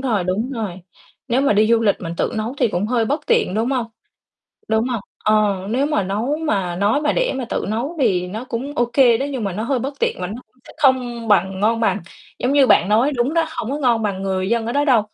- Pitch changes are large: No, average, 4.3 semitones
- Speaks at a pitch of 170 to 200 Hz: No, high, 230 Hz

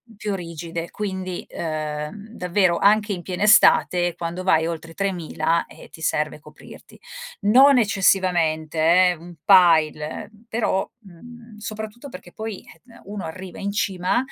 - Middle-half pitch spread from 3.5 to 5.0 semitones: Yes, average, 3.9 semitones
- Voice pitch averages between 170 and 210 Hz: Yes, medium, 185 Hz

